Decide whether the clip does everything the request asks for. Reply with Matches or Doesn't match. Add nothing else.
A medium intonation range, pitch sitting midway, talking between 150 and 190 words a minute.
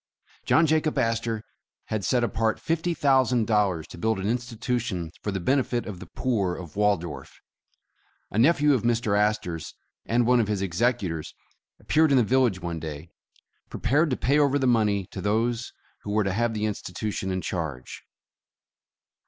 Doesn't match